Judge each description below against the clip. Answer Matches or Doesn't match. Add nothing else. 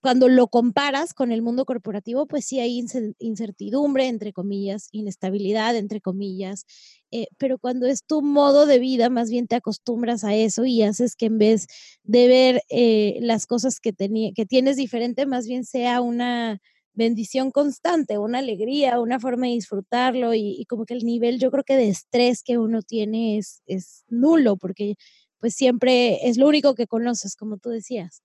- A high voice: Matches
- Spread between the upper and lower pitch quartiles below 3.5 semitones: Matches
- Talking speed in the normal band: Matches